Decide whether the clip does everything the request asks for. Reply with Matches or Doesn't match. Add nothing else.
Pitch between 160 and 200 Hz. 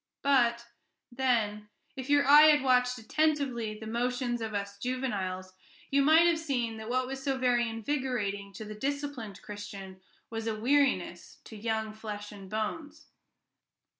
Doesn't match